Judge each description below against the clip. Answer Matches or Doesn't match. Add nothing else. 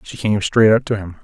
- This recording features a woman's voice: Doesn't match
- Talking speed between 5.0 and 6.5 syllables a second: Matches